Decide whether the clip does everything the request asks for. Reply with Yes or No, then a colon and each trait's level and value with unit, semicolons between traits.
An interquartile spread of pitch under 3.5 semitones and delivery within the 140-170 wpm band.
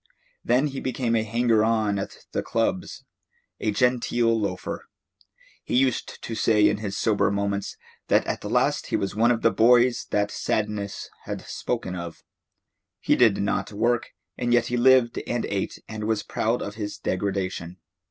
Yes: average, 2.9 semitones; average, 165 wpm